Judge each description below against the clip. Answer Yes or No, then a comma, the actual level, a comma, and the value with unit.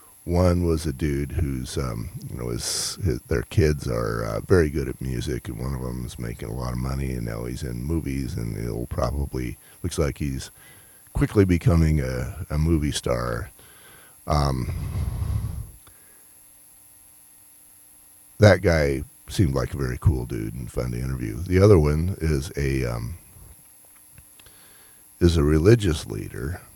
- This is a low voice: Yes, very low, 70 Hz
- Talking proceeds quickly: No, average, 155 wpm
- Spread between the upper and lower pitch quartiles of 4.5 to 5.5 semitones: Yes, average, 5.0 semitones